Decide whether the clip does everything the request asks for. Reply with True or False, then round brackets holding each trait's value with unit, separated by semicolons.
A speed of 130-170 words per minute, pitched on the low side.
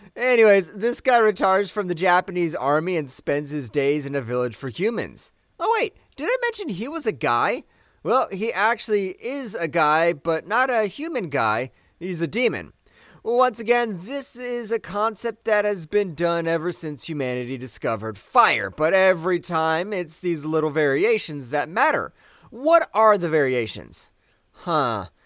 False (165 wpm; 185 Hz)